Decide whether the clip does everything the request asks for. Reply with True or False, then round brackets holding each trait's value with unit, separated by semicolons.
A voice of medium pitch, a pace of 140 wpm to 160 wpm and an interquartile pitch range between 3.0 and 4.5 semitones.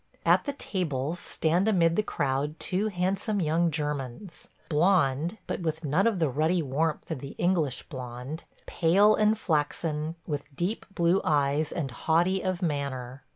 True (160 Hz; 155 wpm; 4.2 semitones)